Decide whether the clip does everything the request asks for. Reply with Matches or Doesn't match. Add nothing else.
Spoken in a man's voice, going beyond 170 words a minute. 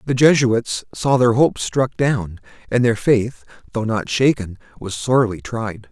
Doesn't match